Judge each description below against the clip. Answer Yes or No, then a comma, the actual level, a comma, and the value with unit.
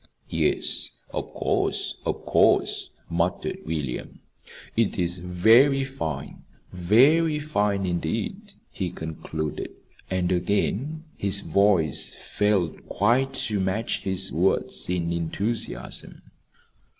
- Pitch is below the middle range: Yes, low, 100 Hz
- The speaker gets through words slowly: Yes, slow, 100 wpm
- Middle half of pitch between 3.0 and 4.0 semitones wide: No, average, 5.0 semitones